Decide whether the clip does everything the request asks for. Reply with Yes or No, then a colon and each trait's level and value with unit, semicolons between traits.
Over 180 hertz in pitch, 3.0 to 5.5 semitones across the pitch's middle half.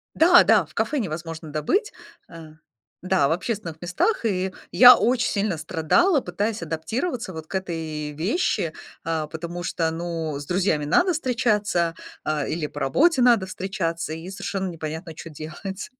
No: medium, 175 Hz; average, 5.0 semitones